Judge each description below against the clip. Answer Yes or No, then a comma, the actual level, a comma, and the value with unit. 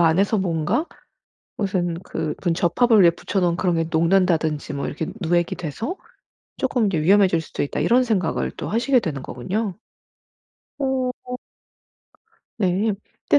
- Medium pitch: Yes, medium, 180 Hz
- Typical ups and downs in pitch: Yes, average, 4.8 semitones